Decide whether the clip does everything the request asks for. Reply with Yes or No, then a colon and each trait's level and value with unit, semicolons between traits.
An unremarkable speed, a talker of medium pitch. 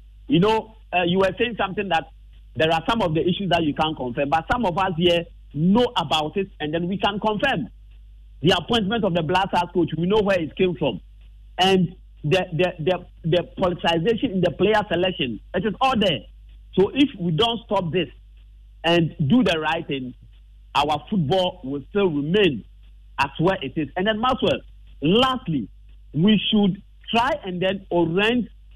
Yes: average, 185 wpm; medium, 180 Hz